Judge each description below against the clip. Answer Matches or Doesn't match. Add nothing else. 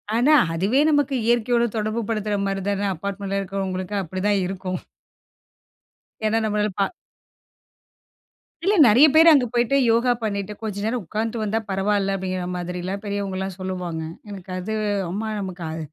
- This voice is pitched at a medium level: Doesn't match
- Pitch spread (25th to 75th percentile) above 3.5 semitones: Doesn't match